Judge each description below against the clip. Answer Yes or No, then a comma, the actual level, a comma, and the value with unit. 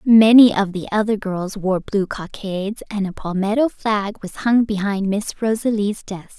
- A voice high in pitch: Yes, high, 205 Hz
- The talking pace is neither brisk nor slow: Yes, average, 170 wpm